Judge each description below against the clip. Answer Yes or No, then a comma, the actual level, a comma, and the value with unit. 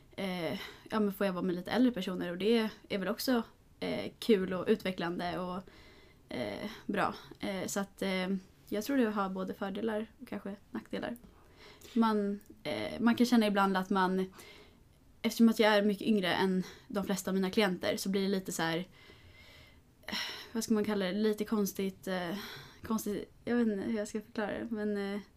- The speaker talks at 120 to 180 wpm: No, average, 190 wpm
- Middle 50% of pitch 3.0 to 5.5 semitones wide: No, narrow, 2.5 semitones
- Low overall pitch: No, high, 205 Hz